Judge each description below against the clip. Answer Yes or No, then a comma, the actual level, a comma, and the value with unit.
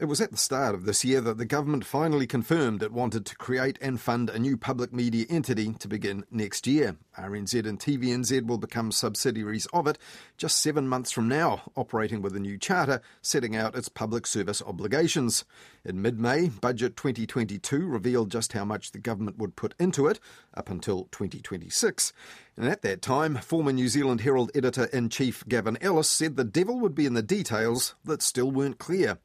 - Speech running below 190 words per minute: No, average, 195 wpm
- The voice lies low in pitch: Yes, low, 125 Hz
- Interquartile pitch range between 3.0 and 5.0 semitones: Yes, average, 3.7 semitones